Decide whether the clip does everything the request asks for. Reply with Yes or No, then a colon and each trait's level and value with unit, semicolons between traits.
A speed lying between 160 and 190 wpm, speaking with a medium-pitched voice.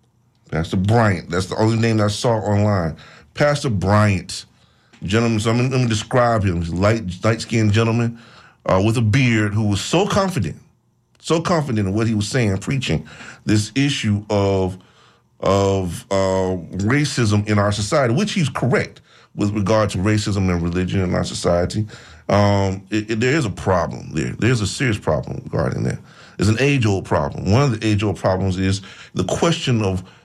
No: average, 175 wpm; low, 105 Hz